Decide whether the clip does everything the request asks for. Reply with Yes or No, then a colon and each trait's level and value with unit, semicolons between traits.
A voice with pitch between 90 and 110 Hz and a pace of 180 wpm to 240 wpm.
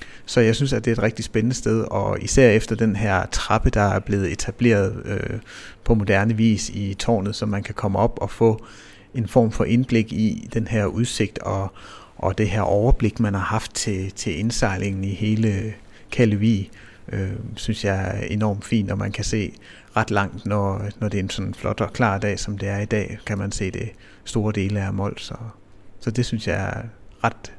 Yes: low, 105 Hz; average, 210 wpm